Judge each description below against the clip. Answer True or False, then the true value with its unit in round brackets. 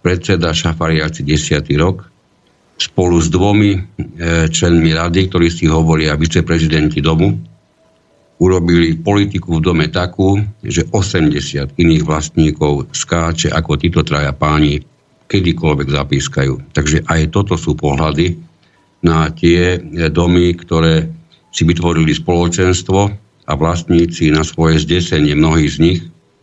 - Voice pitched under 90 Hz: True (80 Hz)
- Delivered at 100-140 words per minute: True (115 wpm)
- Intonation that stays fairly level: True (2.2 semitones)